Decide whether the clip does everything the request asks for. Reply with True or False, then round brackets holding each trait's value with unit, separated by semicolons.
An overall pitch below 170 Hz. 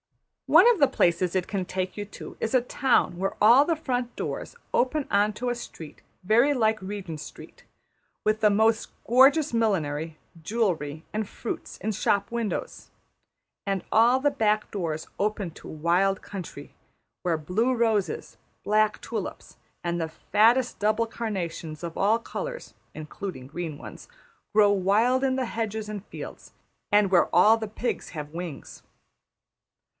False (210 Hz)